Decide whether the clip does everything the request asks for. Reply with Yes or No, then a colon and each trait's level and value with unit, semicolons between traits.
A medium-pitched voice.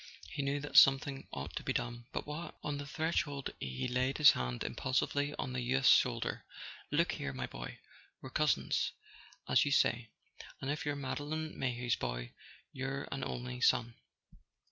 No: low, 130 Hz